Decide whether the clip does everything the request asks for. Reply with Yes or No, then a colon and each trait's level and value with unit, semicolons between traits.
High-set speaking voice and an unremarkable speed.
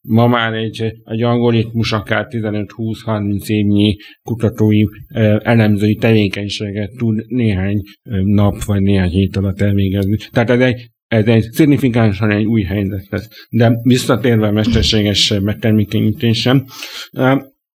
No: low, 110 Hz; average, 120 wpm